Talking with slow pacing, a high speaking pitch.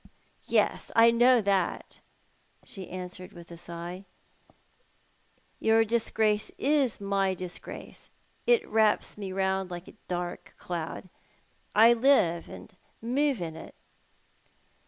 Yes: slow, 120 wpm; high, 195 Hz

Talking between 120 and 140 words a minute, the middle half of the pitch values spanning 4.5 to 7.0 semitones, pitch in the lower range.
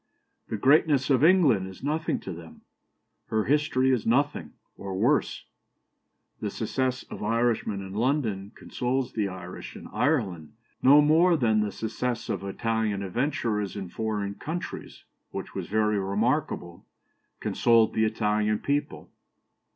Yes: slow, 135 wpm; average, 5.3 semitones; low, 115 Hz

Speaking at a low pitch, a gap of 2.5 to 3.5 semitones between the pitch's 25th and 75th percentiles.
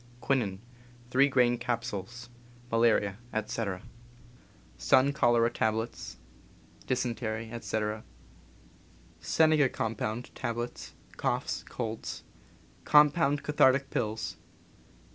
Yes: low, 120 Hz; average, 2.8 semitones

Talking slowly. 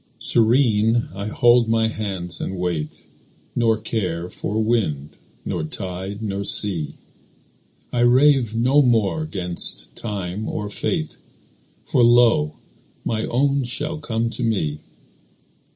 Yes: slow, 120 wpm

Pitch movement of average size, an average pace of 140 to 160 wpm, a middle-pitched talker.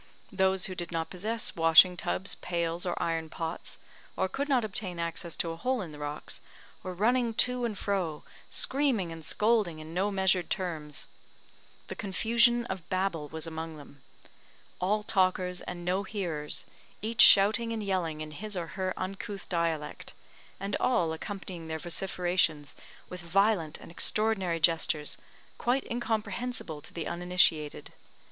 Yes: average, 4.1 semitones; average, 150 wpm; medium, 180 Hz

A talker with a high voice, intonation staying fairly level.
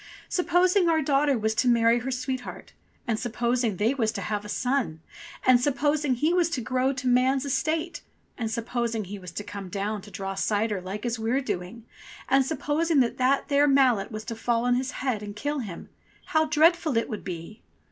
No: high, 245 Hz; average, 4.4 semitones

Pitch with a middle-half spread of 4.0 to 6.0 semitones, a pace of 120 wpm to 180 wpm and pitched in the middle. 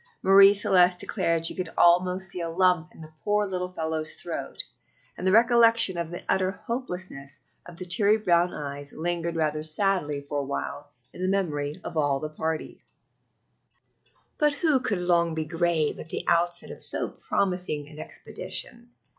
No: average, 3.3 semitones; average, 170 wpm; medium, 175 Hz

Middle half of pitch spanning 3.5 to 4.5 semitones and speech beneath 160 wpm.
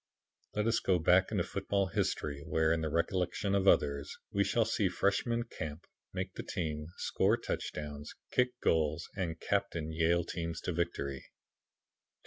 Yes: average, 3.9 semitones; average, 150 wpm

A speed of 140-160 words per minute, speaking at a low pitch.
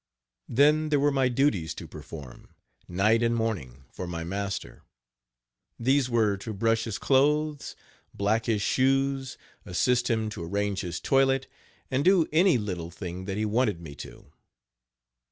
Yes: average, 150 wpm; low, 115 Hz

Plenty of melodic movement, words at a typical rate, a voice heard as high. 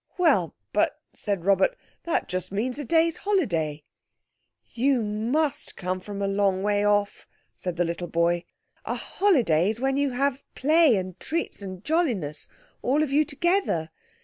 Yes: wide, 8.1 semitones; average, 155 wpm; high, 210 Hz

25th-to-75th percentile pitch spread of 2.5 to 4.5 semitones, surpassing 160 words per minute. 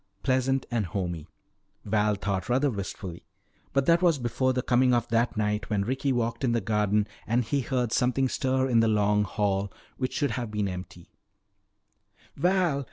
Yes: average, 4.0 semitones; average, 170 wpm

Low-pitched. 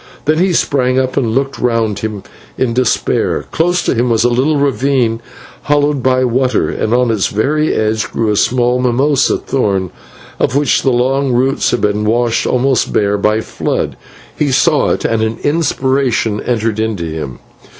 Yes: low, 125 Hz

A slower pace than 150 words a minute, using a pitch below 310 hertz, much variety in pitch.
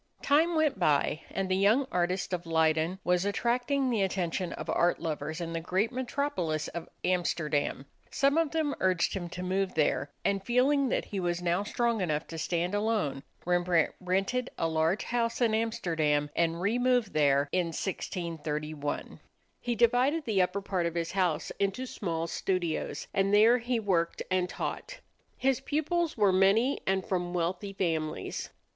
No: average, 165 wpm; medium, 185 Hz; wide, 5.7 semitones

